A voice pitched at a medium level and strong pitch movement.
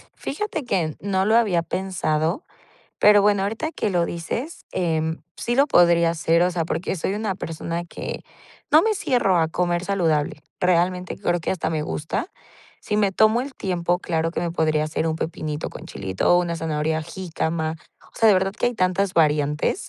No: medium, 175 Hz; average, 3.6 semitones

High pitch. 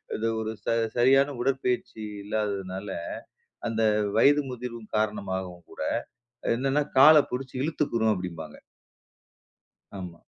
No: low, 115 Hz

